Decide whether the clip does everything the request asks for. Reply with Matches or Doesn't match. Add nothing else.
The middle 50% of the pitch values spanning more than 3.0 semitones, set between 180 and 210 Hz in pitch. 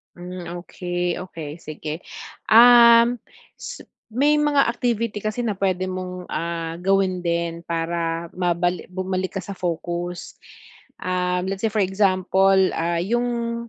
Matches